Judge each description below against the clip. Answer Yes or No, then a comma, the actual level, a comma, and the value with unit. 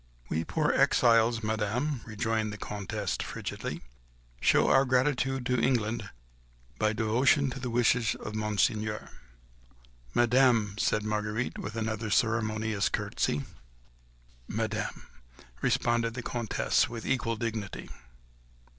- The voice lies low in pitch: Yes, low, 115 Hz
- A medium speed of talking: No, slow, 110 wpm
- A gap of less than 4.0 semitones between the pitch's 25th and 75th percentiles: Yes, narrow, 2.4 semitones